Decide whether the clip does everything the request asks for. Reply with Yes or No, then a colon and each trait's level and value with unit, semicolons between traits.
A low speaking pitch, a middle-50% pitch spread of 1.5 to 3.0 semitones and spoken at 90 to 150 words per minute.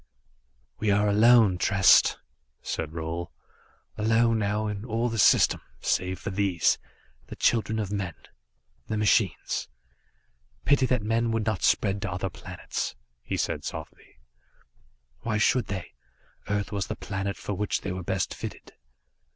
Yes: low, 105 Hz; narrow, 2.6 semitones; average, 145 wpm